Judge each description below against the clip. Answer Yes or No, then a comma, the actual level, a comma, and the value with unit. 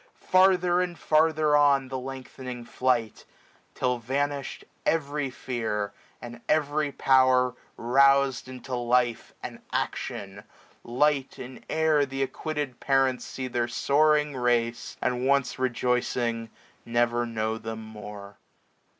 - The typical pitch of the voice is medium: No, low, 130 Hz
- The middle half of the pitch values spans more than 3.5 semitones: No, average, 3.1 semitones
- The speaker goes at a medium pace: No, slow, 115 wpm